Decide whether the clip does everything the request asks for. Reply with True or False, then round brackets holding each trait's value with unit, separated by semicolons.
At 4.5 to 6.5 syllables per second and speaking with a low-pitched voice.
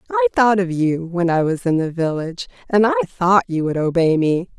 False (5.5 syllables/s; 170 Hz)